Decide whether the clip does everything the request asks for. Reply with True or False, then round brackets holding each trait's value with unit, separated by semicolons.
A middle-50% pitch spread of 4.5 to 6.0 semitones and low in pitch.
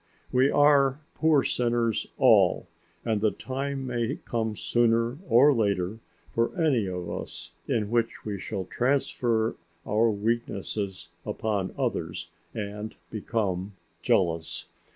False (3.4 semitones; 115 Hz)